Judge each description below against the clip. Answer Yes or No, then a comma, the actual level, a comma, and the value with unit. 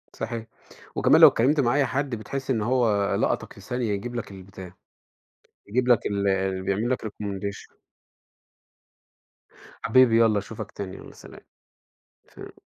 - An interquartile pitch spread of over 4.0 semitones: No, average, 3.7 semitones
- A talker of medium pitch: No, low, 110 Hz